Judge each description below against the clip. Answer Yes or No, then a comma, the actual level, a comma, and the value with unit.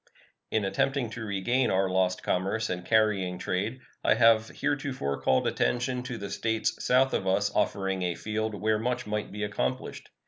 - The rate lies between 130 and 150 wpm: No, average, 170 wpm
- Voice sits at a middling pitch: No, low, 105 Hz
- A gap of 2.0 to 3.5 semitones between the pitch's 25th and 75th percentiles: No, average, 3.9 semitones